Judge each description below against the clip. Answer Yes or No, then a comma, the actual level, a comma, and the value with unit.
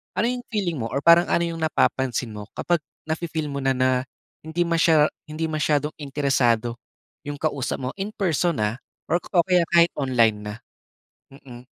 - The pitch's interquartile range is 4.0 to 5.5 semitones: Yes, average, 4.6 semitones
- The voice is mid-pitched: Yes, medium, 150 Hz